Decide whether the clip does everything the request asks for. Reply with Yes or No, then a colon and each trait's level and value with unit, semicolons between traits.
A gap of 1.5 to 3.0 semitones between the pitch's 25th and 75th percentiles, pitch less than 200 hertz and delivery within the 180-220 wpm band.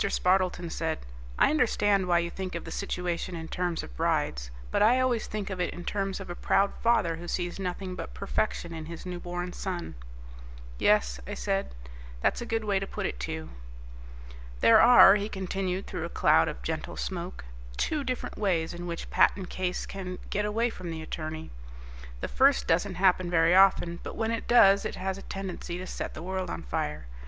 Yes: narrow, 2.6 semitones; medium, 185 Hz; average, 200 wpm